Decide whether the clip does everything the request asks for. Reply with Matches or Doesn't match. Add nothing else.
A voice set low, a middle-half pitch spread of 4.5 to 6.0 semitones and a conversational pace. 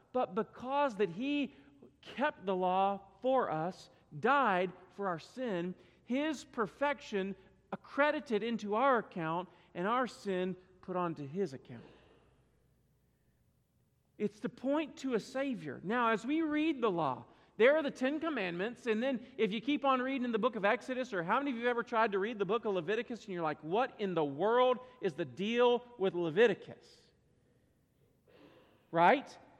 Doesn't match